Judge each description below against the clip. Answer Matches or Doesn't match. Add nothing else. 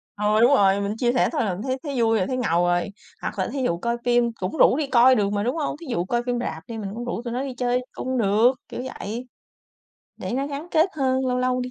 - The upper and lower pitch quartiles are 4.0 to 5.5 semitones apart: Doesn't match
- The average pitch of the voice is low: Doesn't match